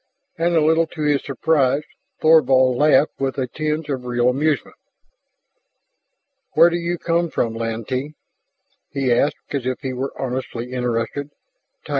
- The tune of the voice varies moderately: Yes, average, 3.7 semitones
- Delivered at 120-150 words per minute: Yes, average, 145 wpm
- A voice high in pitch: No, medium, 140 Hz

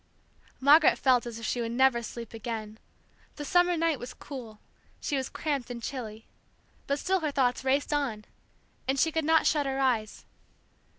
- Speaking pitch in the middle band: No, very high, 265 Hz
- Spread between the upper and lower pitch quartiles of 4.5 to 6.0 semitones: No, average, 3.9 semitones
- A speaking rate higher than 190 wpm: No, average, 175 wpm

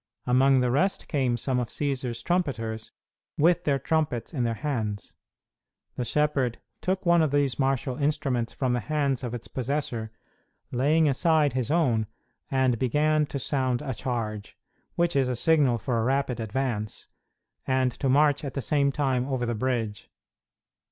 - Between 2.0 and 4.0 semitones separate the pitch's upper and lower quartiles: Yes, average, 3.3 semitones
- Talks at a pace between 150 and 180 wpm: Yes, average, 160 wpm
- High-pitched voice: No, low, 130 Hz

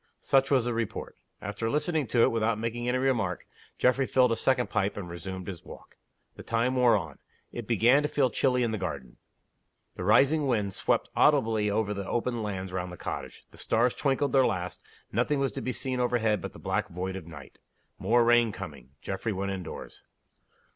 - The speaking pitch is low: Yes, low, 115 Hz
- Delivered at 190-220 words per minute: Yes, average, 195 wpm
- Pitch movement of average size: Yes, average, 4.7 semitones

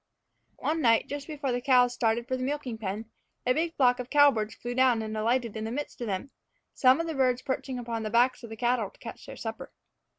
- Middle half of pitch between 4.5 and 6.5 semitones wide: No, average, 2.7 semitones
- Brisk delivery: Yes, fast, 235 wpm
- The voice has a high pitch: Yes, high, 245 Hz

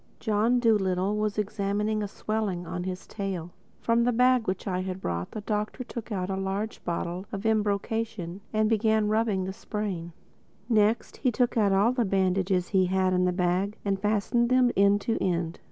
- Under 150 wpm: No, average, 175 wpm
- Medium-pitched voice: No, high, 205 Hz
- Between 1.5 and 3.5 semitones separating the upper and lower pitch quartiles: Yes, average, 2.8 semitones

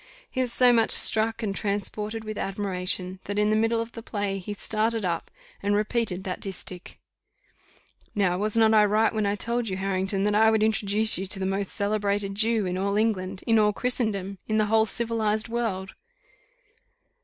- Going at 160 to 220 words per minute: Yes, average, 190 wpm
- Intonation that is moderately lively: No, narrow, 2.2 semitones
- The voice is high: Yes, high, 210 Hz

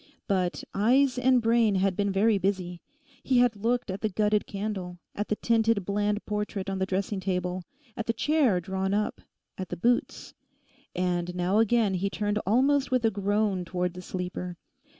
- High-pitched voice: Yes, high, 205 Hz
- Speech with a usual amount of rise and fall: Yes, average, 3.3 semitones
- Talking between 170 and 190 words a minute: Yes, average, 175 wpm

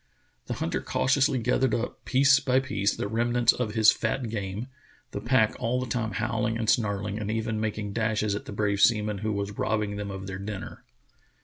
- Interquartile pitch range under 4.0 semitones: Yes, average, 2.7 semitones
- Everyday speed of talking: Yes, average, 195 wpm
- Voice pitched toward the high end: No, low, 110 Hz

